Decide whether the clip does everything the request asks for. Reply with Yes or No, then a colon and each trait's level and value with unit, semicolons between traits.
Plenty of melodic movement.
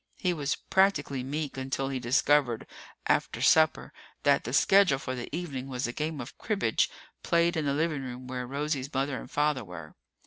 No: average, 3.2 semitones